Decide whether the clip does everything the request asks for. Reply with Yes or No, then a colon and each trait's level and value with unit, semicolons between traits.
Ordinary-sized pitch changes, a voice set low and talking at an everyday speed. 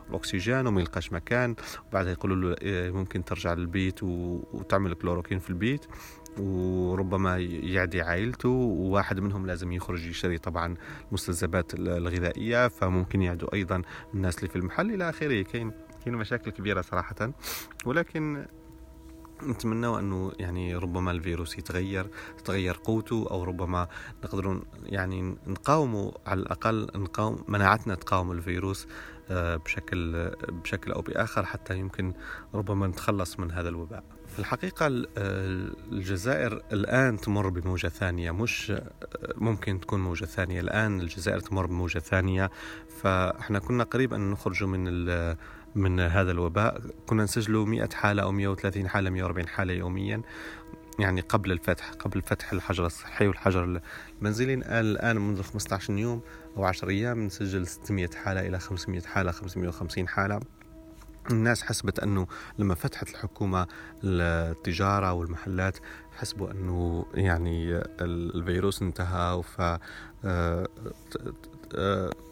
Yes: average, 3.1 semitones; very low, 95 Hz; average, 120 wpm